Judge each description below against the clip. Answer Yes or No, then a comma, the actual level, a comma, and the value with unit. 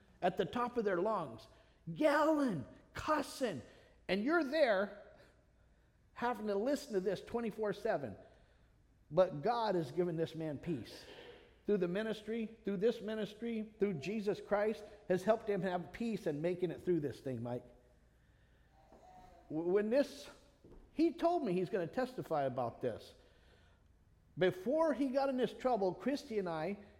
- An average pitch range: No, wide, 5.7 semitones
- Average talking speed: Yes, average, 145 wpm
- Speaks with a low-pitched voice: No, high, 205 Hz